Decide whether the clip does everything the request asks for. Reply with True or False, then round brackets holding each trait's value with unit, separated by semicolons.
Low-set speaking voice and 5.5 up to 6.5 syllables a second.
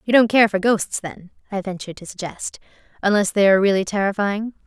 False (200 Hz; 6.0 syllables/s)